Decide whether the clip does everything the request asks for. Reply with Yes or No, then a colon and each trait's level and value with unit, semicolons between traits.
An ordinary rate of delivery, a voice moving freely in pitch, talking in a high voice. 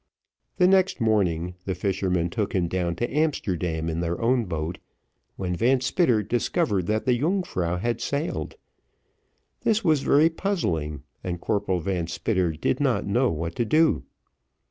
No: average, 150 wpm; wide, 7.7 semitones; low, 100 Hz